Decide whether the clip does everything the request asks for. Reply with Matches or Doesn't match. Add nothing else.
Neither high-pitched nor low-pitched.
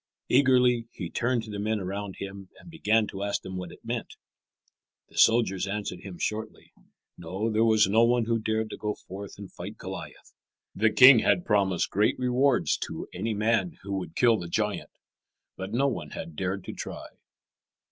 Doesn't match